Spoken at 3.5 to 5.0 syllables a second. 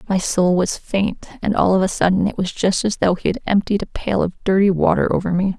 No: 5.5 syllables/s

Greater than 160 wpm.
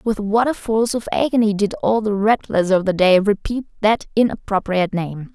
Yes: average, 190 wpm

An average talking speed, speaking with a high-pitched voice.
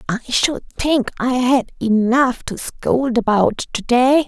Yes: average, 155 wpm; high, 245 Hz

